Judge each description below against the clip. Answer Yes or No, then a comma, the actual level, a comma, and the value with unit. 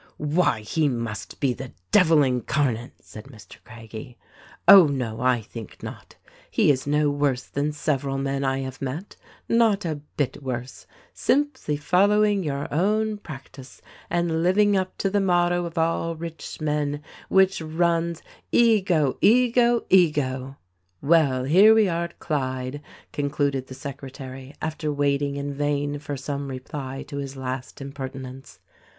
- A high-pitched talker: No, medium, 145 Hz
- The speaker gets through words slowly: No, average, 145 wpm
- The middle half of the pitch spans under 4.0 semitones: No, average, 4.4 semitones